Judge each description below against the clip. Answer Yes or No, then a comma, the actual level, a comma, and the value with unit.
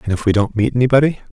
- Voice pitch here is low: Yes, low, 115 Hz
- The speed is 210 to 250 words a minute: No, fast, 260 wpm